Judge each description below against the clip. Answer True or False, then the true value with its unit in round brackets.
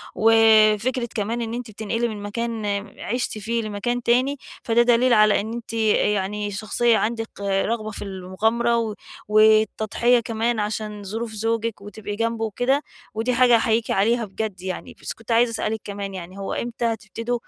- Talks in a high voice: True (220 Hz)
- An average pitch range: False (2.0 semitones)